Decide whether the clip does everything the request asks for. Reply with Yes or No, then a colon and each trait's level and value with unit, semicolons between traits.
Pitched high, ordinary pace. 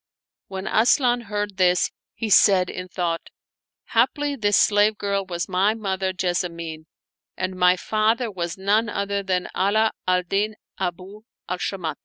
Yes: high, 195 Hz; average, 150 wpm